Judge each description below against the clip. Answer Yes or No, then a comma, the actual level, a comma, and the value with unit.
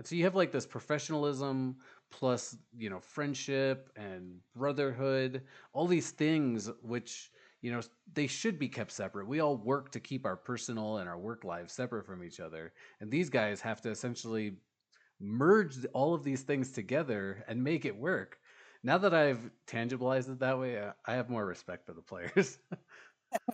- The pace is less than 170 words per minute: No, average, 175 wpm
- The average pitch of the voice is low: Yes, low, 125 Hz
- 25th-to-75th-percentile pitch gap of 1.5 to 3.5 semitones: No, average, 4.0 semitones